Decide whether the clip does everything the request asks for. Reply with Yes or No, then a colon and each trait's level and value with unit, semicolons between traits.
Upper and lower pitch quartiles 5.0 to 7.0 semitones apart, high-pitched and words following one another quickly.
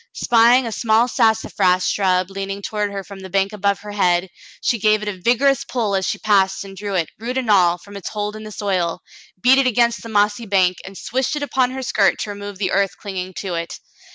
No: average, 3.0 semitones; high, 205 Hz; fast, 235 wpm